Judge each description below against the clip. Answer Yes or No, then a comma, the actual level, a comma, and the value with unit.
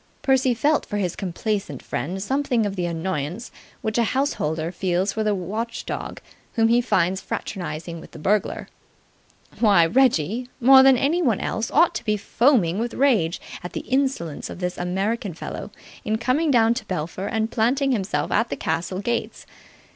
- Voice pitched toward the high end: Yes, high, 215 Hz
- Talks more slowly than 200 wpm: Yes, average, 165 wpm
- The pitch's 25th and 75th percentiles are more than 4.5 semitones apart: Yes, wide, 5.5 semitones